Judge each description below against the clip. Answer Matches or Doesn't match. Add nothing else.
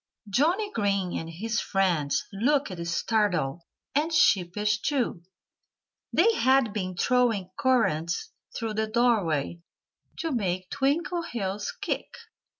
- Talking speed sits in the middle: Doesn't match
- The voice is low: Doesn't match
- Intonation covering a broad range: Matches